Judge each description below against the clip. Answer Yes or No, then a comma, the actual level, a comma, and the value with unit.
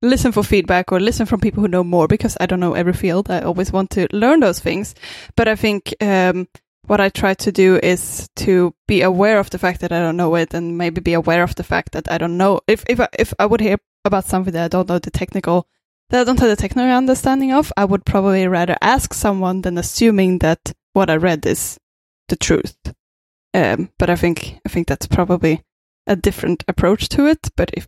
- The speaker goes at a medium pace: No, fast, 230 wpm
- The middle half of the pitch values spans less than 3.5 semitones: Yes, average, 3.1 semitones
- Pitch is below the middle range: No, medium, 185 Hz